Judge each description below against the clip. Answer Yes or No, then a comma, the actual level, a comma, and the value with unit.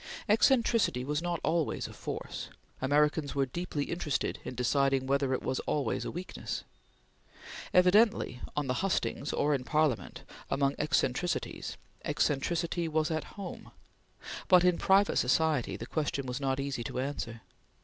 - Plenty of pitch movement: No, average, 4.4 semitones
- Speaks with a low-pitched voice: No, medium, 145 Hz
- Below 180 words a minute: Yes, average, 140 wpm